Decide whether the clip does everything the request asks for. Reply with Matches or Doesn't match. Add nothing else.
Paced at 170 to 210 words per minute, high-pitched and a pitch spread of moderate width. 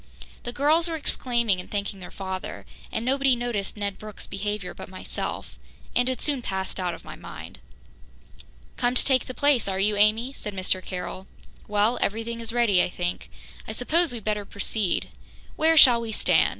Matches